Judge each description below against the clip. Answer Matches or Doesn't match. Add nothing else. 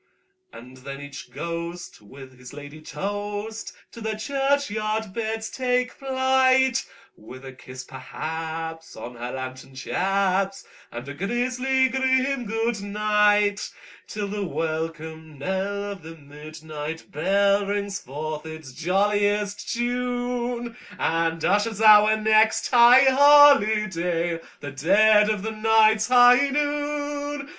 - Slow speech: Matches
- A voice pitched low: Doesn't match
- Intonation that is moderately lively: Doesn't match